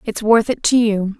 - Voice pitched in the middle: No, high, 220 Hz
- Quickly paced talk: Yes, fast, 250 wpm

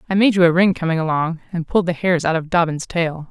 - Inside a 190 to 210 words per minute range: No, fast, 275 wpm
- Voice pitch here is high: No, medium, 170 Hz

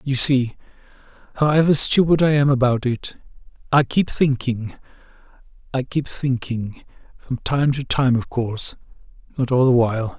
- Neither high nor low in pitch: No, low, 130 Hz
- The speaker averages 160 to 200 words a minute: No, slow, 135 wpm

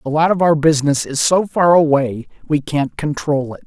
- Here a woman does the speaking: No, male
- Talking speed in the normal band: No, fast, 215 wpm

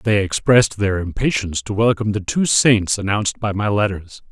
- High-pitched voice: No, low, 105 Hz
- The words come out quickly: No, average, 180 wpm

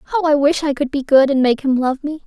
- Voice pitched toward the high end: Yes, very high, 280 Hz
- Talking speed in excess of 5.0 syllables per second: Yes, 5.5 syllables/s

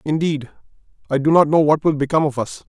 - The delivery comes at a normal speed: Yes, average, 195 wpm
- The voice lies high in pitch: No, medium, 150 Hz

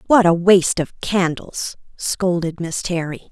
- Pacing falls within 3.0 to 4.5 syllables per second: Yes, 4.1 syllables/s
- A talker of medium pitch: Yes, medium, 175 Hz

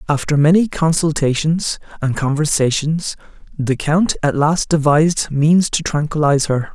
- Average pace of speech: No, slow, 125 wpm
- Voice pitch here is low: No, medium, 150 Hz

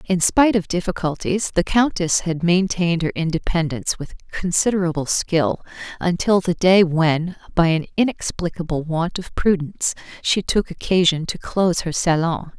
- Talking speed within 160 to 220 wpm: No, average, 145 wpm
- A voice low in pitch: No, medium, 175 Hz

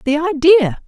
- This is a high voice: Yes, very high, 305 Hz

